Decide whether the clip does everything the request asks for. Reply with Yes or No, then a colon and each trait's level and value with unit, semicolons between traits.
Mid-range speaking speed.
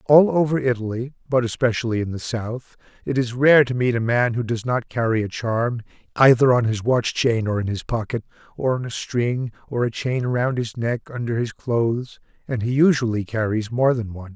No: fast, 210 wpm